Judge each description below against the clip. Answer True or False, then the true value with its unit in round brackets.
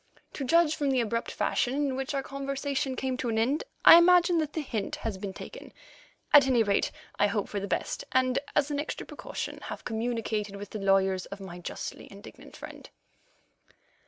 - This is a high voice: True (255 Hz)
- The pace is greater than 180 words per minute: True (190 wpm)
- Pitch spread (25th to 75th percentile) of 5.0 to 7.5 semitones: True (5.6 semitones)